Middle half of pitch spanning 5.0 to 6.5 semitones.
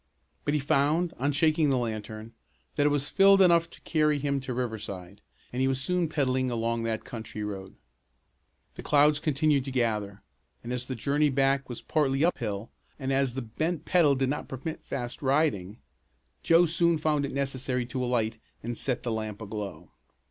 No: average, 4.3 semitones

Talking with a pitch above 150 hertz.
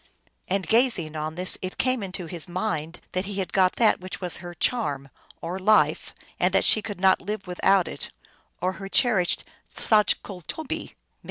Yes: medium, 185 Hz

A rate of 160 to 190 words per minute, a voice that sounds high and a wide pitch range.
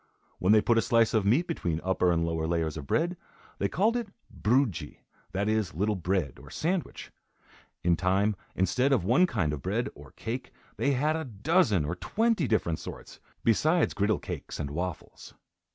No: average, 180 wpm; low, 105 Hz; wide, 8.0 semitones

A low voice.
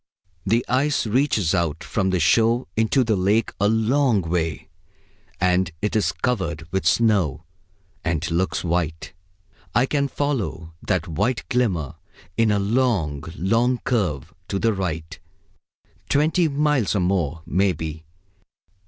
Yes: low, 100 Hz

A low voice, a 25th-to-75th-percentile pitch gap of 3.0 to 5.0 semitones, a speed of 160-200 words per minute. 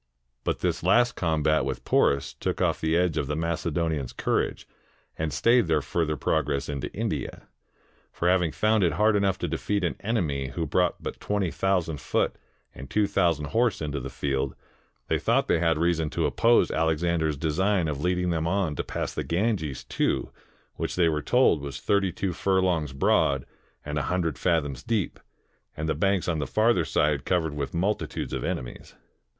Yes: very low, 80 Hz; average, 3.9 semitones; average, 180 wpm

